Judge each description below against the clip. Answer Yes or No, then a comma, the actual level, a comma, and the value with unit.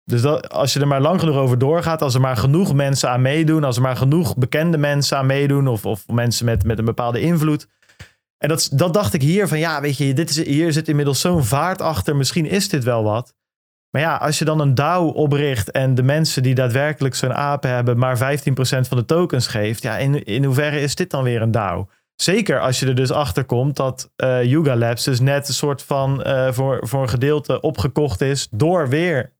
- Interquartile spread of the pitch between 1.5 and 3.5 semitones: Yes, average, 2.8 semitones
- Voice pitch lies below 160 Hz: Yes, medium, 140 Hz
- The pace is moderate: No, fast, 230 wpm